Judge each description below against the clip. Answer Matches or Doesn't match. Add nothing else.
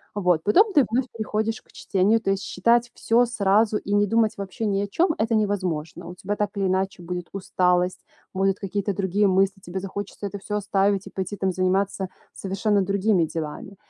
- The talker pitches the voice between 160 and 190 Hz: Doesn't match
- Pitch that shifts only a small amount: Matches